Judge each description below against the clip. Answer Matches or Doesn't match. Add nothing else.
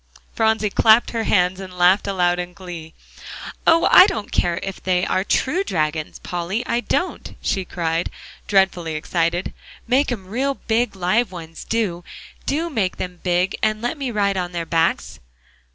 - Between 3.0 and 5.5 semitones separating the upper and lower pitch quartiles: Matches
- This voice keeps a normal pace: Matches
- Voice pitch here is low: Doesn't match